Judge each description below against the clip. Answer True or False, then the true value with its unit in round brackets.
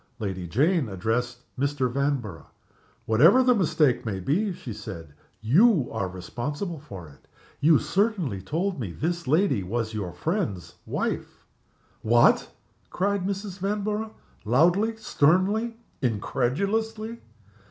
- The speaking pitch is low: False (145 Hz)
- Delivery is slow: True (115 wpm)